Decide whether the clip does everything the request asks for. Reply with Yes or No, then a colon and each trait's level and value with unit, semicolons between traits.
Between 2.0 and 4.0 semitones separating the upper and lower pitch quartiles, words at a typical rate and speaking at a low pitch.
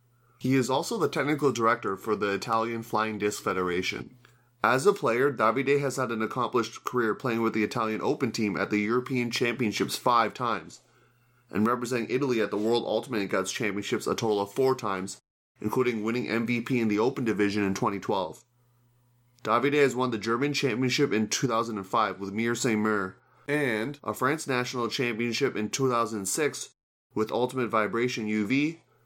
Yes: average, 3.1 semitones; average, 160 wpm; low, 120 Hz